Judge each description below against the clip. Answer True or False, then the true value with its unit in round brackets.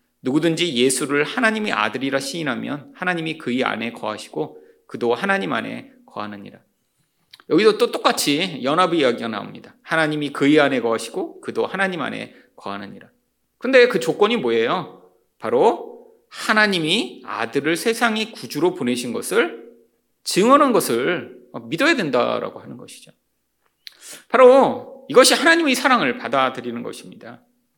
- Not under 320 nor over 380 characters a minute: True (330 characters per minute)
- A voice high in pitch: True (215 Hz)